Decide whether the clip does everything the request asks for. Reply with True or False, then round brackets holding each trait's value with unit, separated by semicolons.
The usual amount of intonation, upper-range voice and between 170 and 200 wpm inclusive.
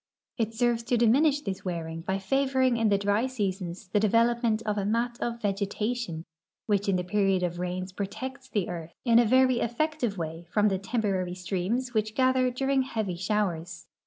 True (4.4 semitones; 210 Hz; 185 wpm)